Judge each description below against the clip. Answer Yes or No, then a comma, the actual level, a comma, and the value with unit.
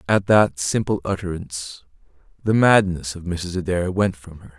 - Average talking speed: Yes, average, 155 wpm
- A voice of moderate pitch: No, very low, 90 Hz